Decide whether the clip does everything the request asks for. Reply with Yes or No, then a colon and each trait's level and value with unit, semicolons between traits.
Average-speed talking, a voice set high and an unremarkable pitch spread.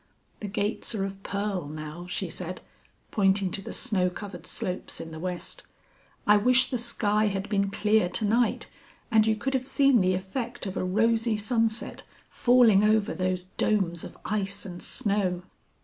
Yes: average, 170 wpm; high, 205 Hz; average, 3.0 semitones